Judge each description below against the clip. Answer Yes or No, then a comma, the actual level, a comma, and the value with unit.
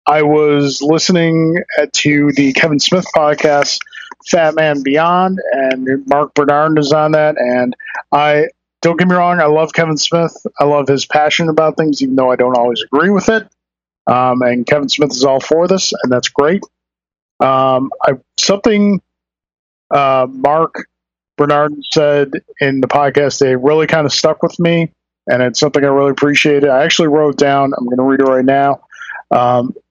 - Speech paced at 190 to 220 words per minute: No, average, 175 wpm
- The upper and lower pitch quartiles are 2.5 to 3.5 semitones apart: Yes, average, 3.0 semitones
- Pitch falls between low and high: Yes, medium, 145 Hz